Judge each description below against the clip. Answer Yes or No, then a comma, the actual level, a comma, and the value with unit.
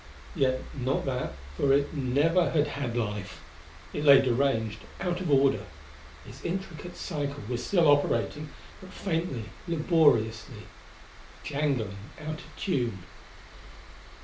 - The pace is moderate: No, slow, 120 wpm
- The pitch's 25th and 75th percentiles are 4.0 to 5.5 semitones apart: Yes, average, 4.4 semitones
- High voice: No, medium, 140 Hz